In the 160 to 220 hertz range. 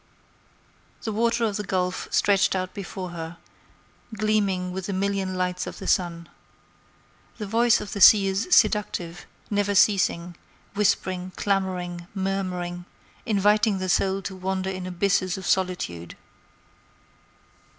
Yes: high, 190 Hz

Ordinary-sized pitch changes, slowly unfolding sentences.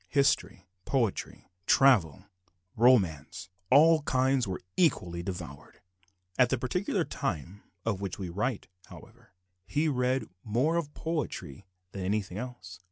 No: wide, 6.7 semitones; slow, 125 wpm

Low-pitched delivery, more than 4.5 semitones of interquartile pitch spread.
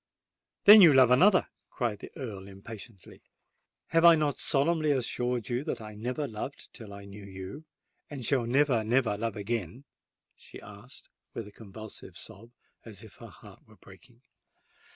Yes: low, 120 Hz; average, 5.1 semitones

